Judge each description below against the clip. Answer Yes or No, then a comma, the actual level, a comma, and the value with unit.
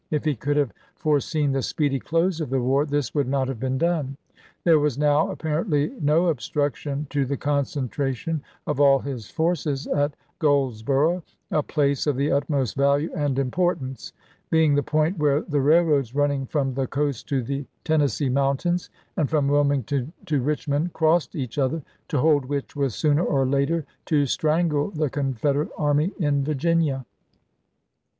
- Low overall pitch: No, medium, 145 Hz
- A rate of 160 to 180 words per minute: Yes, average, 170 wpm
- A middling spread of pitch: No, narrow, 2.2 semitones